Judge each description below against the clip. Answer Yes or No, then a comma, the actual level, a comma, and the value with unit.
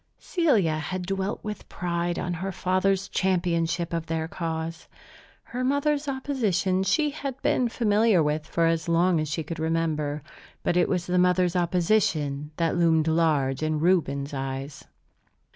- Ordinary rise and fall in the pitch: Yes, average, 3.3 semitones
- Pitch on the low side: No, medium, 175 Hz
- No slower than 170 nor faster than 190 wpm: No, average, 150 wpm